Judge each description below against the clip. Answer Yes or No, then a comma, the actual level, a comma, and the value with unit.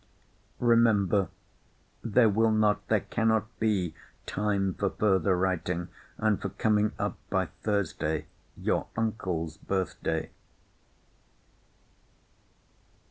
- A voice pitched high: No, low, 100 Hz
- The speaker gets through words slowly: Yes, slow, 95 wpm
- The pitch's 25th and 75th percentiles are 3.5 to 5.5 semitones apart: No, average, 2.7 semitones